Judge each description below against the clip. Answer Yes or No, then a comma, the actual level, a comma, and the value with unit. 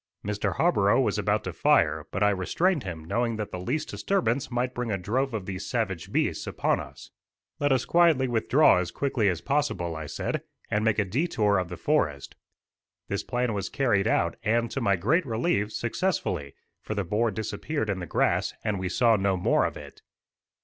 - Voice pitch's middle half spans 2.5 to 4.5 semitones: No, average, 5.1 semitones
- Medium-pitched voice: No, low, 110 Hz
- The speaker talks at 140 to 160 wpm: No, average, 195 wpm